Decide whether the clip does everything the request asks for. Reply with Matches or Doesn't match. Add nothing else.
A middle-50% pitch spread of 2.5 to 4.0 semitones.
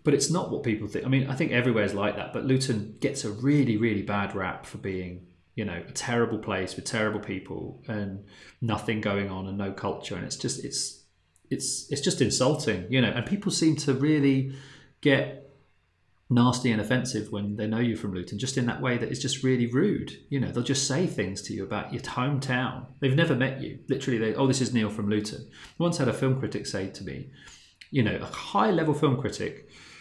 Doesn't match